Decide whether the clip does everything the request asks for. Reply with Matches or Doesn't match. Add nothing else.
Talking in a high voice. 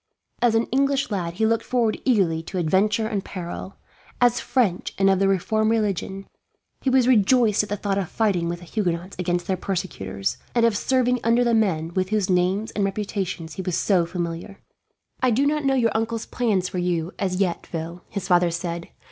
Matches